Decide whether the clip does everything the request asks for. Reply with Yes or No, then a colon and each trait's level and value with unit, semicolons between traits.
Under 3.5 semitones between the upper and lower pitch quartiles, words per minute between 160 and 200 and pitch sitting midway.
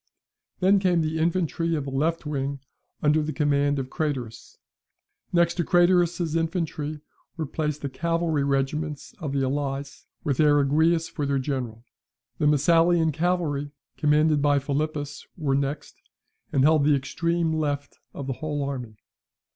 No: narrow, 2.6 semitones; average, 145 wpm; medium, 150 Hz